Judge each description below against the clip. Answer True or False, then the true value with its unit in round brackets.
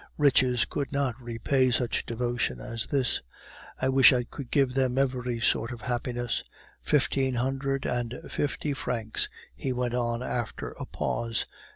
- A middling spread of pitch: False (2.0 semitones)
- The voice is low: True (125 Hz)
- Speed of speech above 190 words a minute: False (150 wpm)